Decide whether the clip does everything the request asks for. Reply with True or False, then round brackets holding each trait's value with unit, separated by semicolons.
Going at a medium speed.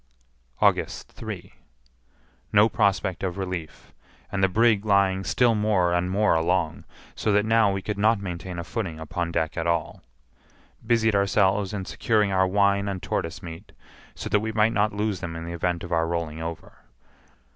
True (175 wpm)